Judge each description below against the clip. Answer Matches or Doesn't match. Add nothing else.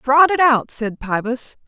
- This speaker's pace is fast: Doesn't match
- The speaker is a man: Doesn't match